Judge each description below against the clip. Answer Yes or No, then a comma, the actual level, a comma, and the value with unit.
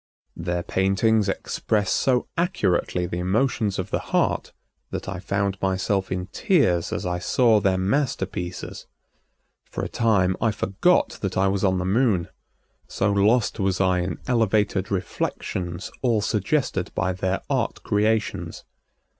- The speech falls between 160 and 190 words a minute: No, average, 140 wpm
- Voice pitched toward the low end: Yes, very low, 95 Hz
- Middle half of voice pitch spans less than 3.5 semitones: Yes, average, 2.8 semitones